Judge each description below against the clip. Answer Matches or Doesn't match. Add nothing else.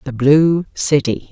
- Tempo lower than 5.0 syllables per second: Matches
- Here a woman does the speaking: Matches